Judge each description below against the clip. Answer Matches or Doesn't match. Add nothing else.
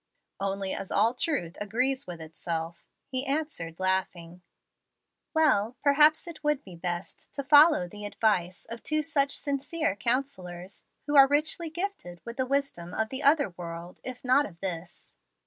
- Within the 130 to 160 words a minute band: Matches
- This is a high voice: Matches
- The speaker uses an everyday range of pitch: Doesn't match